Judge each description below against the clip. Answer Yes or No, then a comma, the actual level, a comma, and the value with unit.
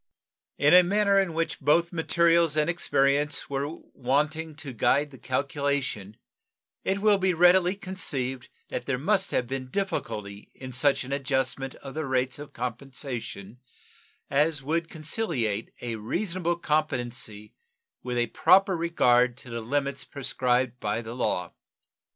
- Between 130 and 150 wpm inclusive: Yes, average, 140 wpm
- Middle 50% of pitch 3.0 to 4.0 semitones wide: No, average, 5.0 semitones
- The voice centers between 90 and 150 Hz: Yes, medium, 140 Hz